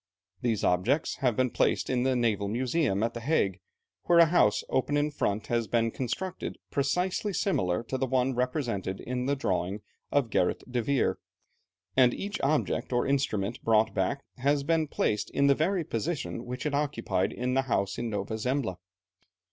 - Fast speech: No, average, 175 wpm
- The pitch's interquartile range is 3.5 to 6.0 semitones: Yes, average, 4.3 semitones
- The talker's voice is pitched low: Yes, low, 125 Hz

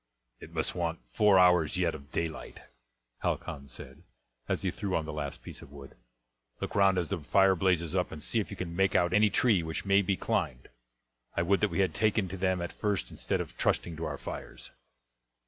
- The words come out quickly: Yes, fast, 215 wpm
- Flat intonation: No, average, 3.4 semitones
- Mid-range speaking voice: No, very low, 90 Hz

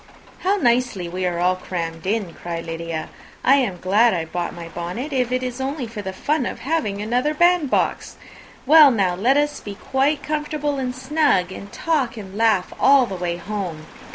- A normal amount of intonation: No, wide, 7.3 semitones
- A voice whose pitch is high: Yes, high, 225 Hz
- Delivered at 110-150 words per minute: No, average, 185 wpm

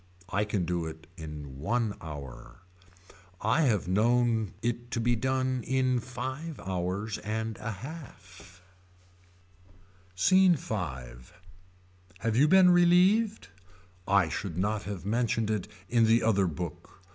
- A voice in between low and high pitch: No, low, 110 Hz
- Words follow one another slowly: Yes, slow, 125 wpm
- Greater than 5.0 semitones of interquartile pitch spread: Yes, wide, 5.6 semitones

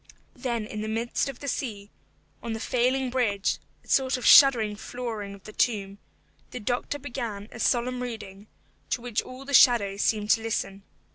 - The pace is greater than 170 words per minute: Yes, average, 180 wpm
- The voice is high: Yes, high, 235 Hz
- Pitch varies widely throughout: No, average, 3.2 semitones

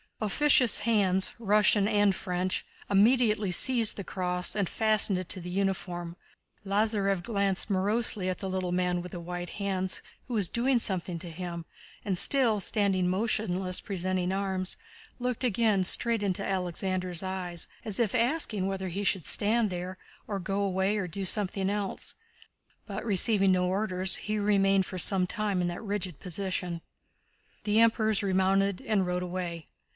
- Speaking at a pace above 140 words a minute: Yes, average, 155 wpm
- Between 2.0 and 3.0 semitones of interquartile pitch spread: Yes, narrow, 2.5 semitones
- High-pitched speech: Yes, high, 195 Hz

